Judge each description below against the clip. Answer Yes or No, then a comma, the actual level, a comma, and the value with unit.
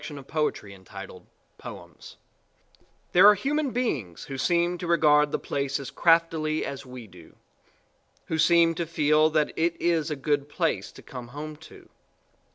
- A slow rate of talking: No, average, 165 wpm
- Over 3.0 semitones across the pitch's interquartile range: Yes, average, 3.4 semitones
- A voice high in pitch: No, medium, 155 Hz